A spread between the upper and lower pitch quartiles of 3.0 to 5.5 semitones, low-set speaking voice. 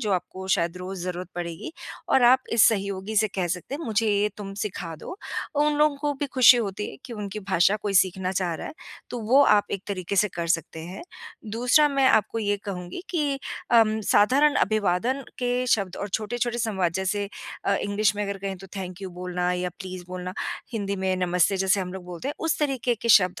No: average, 4.2 semitones; high, 200 Hz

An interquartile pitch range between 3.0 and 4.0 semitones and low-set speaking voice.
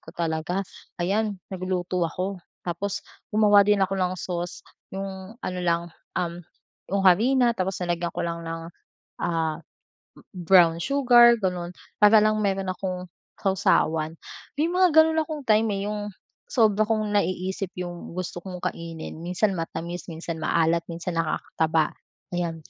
No: average, 3.4 semitones; medium, 185 Hz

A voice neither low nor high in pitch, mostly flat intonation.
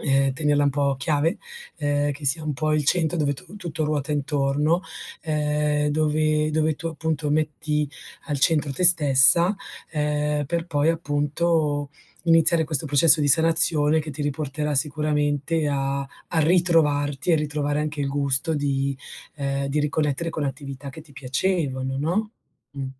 Yes: medium, 150 Hz; narrow, 1.8 semitones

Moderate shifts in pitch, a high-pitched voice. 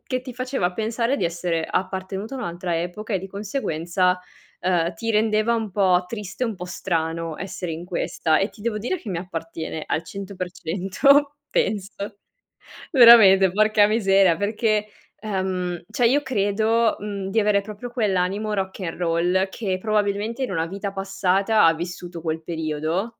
Yes: average, 3.5 semitones; high, 195 Hz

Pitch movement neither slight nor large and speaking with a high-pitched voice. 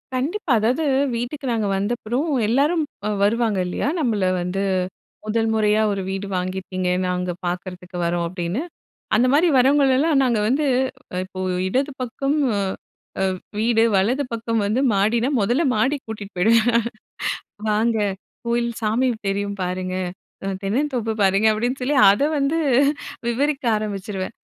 Yes: average, 4.7 semitones; high, 225 Hz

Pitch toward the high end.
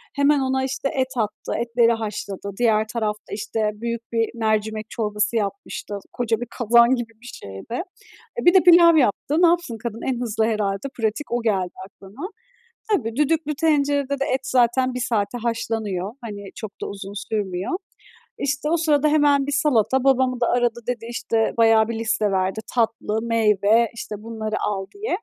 Yes: high, 230 Hz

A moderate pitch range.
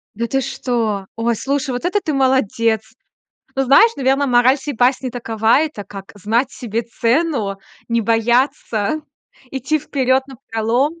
Yes: average, 3.2 semitones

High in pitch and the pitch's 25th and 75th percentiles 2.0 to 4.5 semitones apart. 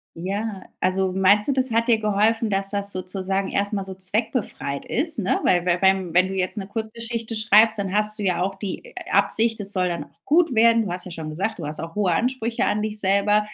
Yes: high, 200 Hz; average, 2.9 semitones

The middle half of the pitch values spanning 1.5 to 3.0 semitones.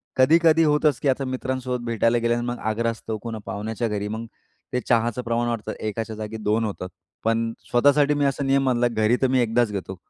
Yes: average, 2.7 semitones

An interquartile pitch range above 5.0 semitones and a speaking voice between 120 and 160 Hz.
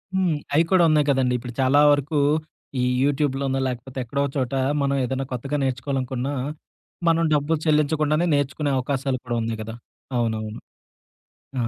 No: average, 2.7 semitones; low, 135 Hz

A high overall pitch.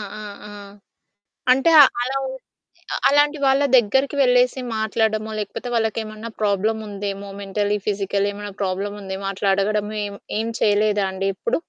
Yes: high, 210 Hz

